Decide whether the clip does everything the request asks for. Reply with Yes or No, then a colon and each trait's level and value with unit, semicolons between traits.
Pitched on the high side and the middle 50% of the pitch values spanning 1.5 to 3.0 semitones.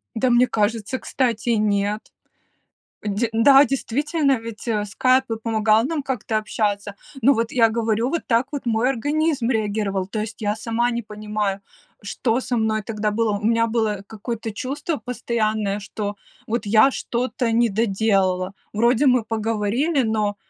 Yes: high, 225 Hz; narrow, 2.5 semitones